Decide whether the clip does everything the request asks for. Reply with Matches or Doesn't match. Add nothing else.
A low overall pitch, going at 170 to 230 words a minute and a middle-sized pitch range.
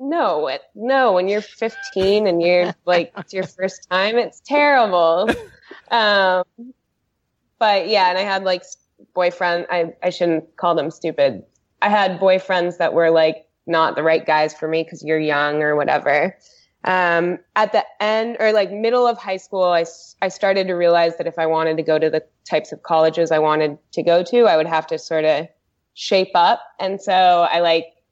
Doesn't match